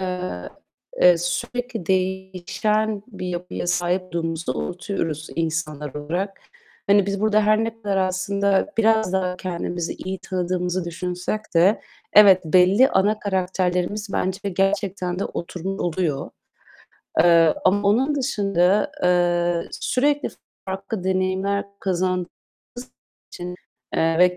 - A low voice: No, medium, 185 Hz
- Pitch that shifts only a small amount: Yes, narrow, 2.3 semitones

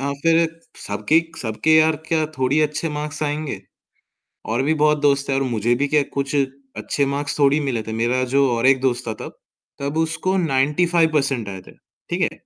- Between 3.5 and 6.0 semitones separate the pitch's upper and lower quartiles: No, average, 3.1 semitones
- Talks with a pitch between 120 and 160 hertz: Yes, medium, 140 Hz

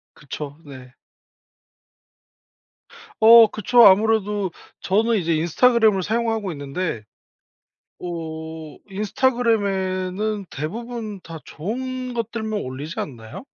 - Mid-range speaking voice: No, high, 195 Hz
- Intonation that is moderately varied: No, wide, 5.8 semitones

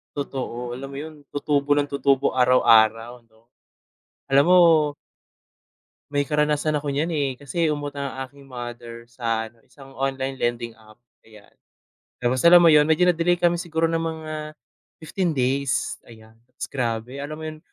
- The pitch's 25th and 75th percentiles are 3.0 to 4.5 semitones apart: Yes, average, 4.1 semitones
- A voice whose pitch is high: No, medium, 140 Hz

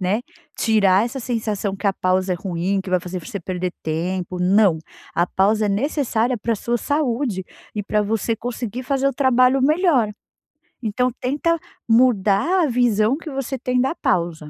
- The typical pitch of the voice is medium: No, high, 220 Hz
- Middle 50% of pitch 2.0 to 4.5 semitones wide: No, average, 5.1 semitones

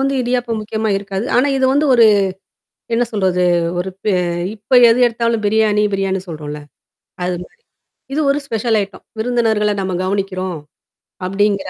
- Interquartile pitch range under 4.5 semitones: Yes, average, 3.5 semitones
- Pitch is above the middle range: Yes, high, 210 Hz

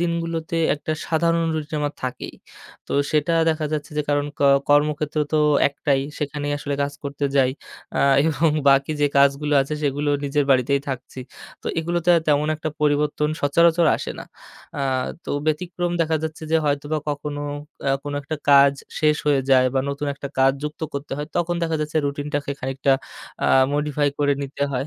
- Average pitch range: No, narrow, 1.9 semitones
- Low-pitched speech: No, medium, 145 Hz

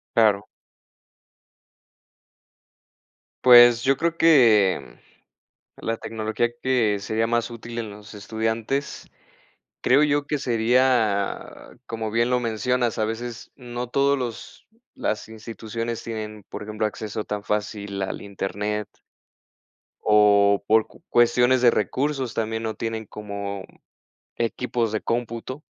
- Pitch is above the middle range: No, low, 115 Hz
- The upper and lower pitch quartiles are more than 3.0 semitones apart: No, narrow, 2.4 semitones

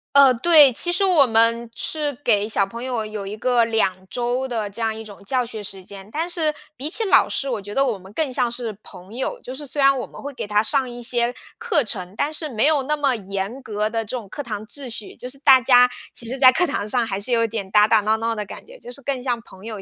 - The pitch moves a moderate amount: Yes, average, 4.3 semitones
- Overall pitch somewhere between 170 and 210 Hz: No, high, 240 Hz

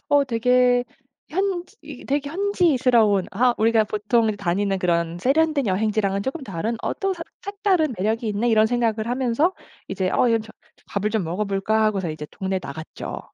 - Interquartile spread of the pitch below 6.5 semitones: Yes, average, 5.2 semitones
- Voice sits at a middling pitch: No, high, 225 Hz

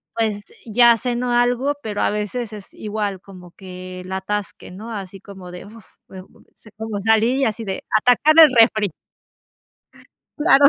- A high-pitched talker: Yes, high, 215 Hz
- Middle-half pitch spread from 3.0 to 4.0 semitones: Yes, average, 3.5 semitones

